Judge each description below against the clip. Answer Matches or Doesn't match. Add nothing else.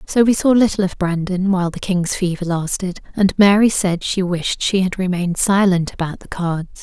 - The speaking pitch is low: Doesn't match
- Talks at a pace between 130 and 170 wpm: Doesn't match